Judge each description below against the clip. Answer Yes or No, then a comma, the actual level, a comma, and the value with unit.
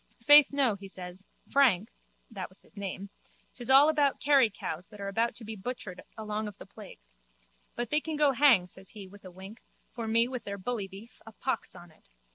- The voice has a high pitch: Yes, high, 215 Hz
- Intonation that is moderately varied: Yes, average, 4.6 semitones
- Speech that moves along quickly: Yes, fast, 210 wpm